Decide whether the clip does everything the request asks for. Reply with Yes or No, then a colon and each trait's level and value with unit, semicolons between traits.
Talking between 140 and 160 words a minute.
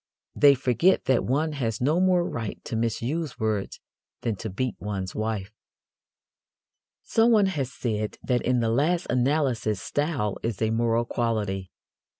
Yes: average, 145 wpm